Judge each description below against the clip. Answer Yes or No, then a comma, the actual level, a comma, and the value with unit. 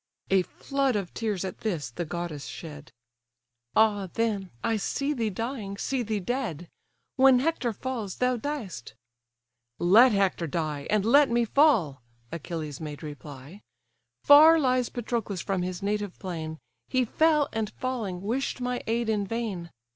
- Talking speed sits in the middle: Yes, average, 145 wpm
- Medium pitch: No, high, 205 Hz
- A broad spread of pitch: Yes, wide, 6.5 semitones